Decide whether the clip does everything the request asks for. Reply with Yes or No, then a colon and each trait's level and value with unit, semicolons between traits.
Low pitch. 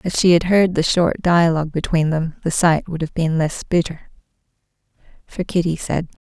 No: medium, 165 Hz